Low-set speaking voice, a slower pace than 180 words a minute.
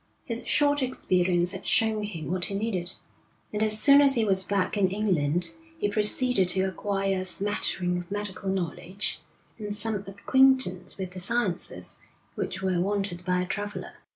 No: high, 195 Hz; average, 165 wpm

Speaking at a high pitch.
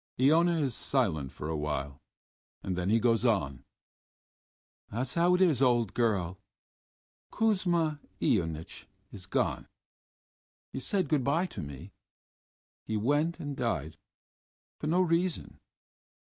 No: low, 120 Hz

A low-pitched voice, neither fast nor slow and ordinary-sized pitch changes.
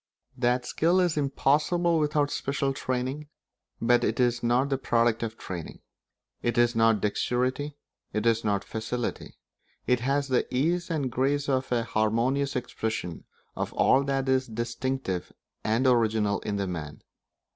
Yes: low, 125 Hz; average, 145 wpm; average, 3.5 semitones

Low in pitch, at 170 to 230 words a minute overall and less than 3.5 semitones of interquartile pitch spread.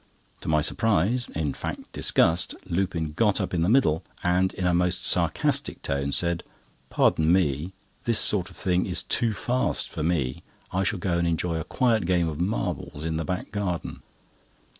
Yes: very low, 90 Hz; average, 180 wpm; average, 3.0 semitones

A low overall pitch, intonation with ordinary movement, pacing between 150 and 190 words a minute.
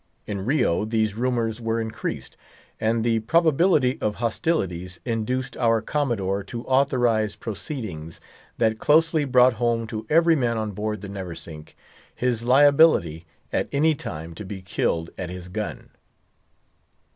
No: low, 115 Hz; average, 4.4 semitones; slow, 135 wpm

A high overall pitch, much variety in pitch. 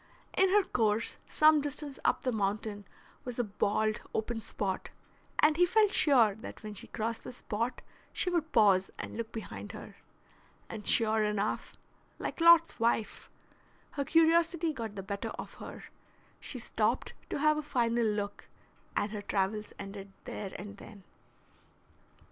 Yes: high, 225 Hz; wide, 6.3 semitones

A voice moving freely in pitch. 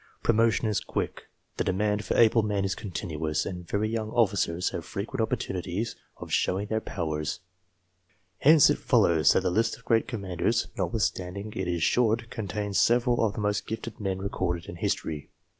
No: average, 3.9 semitones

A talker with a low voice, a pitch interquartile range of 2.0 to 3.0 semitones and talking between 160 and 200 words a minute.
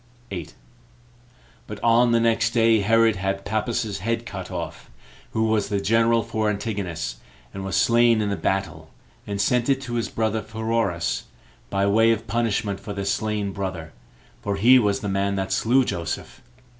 Yes: low, 105 Hz; average, 2.7 semitones; average, 170 wpm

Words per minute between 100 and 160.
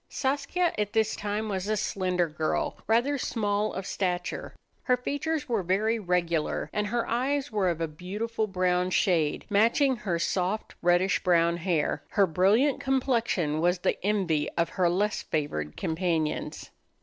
Yes: average, 150 wpm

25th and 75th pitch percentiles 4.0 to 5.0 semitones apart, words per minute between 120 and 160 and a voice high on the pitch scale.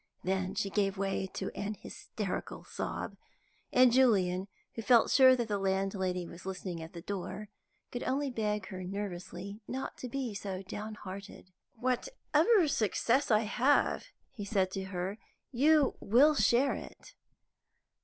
Yes: average, 4.5 semitones; average, 145 wpm; high, 205 Hz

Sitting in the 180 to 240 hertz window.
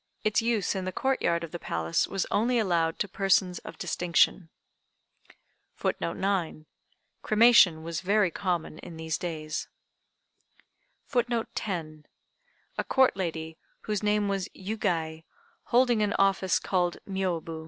Yes: medium, 185 Hz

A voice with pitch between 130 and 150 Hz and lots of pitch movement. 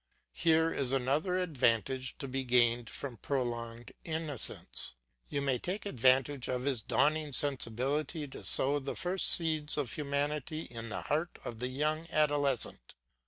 No: medium, 140 Hz; average, 3.6 semitones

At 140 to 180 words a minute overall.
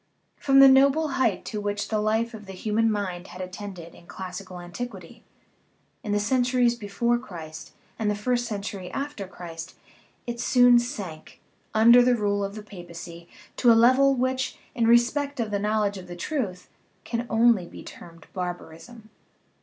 Yes: average, 170 wpm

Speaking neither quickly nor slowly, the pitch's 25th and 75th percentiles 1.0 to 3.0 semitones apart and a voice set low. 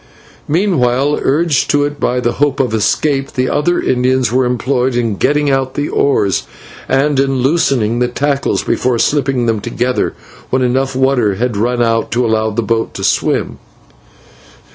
Yes: average, 165 wpm; narrow, 2.6 semitones; low, 130 Hz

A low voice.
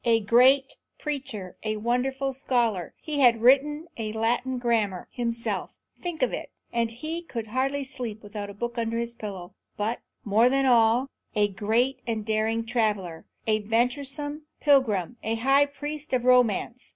No: high, 235 Hz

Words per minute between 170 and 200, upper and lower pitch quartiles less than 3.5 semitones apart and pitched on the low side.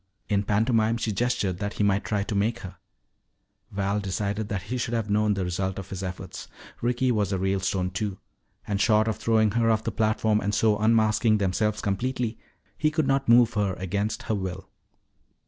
Yes: average, 190 wpm; narrow, 2.4 semitones; low, 105 Hz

